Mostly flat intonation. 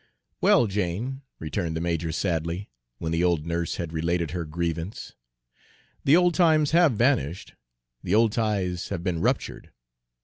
No: average, 5.2 semitones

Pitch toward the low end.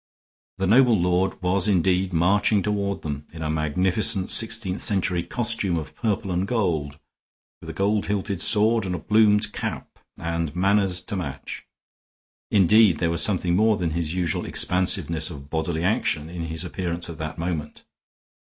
Yes: very low, 90 Hz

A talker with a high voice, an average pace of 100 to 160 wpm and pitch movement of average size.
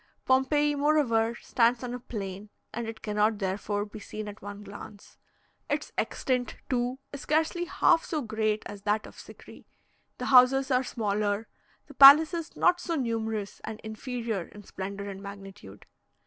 Yes: high, 225 Hz; average, 155 wpm; average, 4.3 semitones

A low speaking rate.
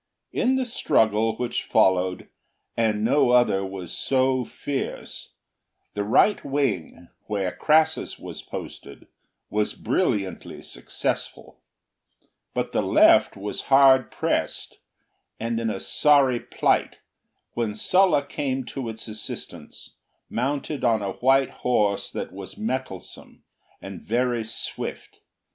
Yes: slow, 115 wpm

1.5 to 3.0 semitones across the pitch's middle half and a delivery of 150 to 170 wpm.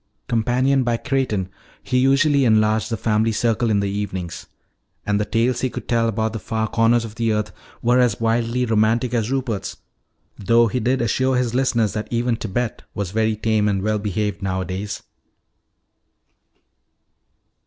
Yes: narrow, 2.5 semitones; average, 160 wpm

